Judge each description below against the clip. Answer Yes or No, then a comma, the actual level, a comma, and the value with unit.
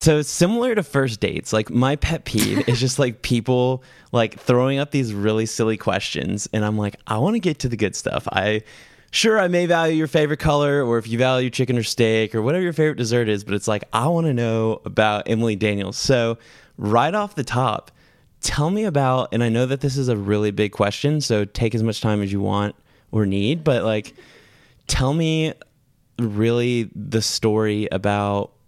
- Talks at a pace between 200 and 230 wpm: Yes, fast, 205 wpm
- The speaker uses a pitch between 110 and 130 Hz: Yes, low, 120 Hz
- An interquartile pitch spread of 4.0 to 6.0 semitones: Yes, average, 4.7 semitones